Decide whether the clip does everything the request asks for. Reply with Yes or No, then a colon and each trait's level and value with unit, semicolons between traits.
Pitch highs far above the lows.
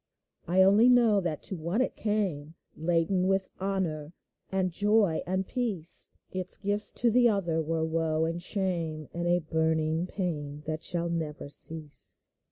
No: average, 3.4 semitones